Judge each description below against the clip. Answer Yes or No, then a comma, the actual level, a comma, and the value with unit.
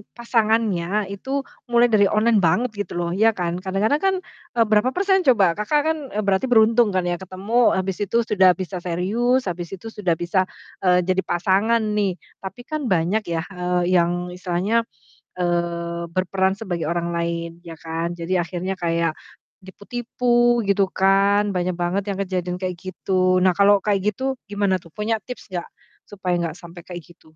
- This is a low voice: No, high, 190 Hz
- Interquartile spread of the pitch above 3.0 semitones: Yes, average, 3.7 semitones